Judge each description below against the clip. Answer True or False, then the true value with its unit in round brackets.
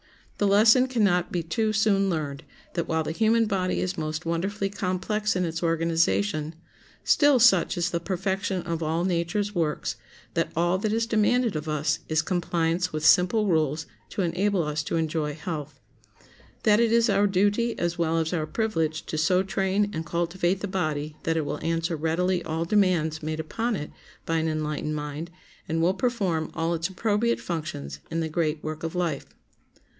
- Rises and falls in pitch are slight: False (3.9 semitones)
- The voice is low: False (170 Hz)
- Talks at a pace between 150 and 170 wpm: False (180 wpm)